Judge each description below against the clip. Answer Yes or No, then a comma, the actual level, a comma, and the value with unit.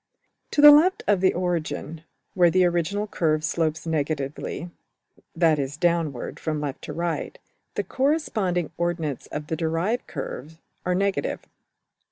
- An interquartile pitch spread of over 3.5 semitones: No, average, 3.1 semitones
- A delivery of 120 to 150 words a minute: Yes, average, 140 wpm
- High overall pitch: No, medium, 170 Hz